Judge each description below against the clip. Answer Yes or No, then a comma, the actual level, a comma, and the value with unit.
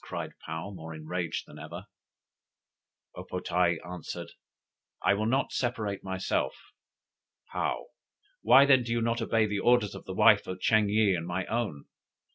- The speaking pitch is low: Yes, low, 100 Hz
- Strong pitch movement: No, average, 4.3 semitones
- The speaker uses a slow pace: No, average, 160 wpm